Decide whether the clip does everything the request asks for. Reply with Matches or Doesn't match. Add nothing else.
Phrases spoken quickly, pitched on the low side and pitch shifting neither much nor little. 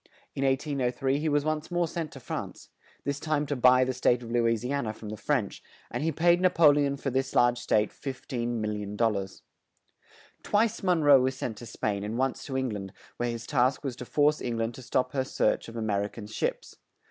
Matches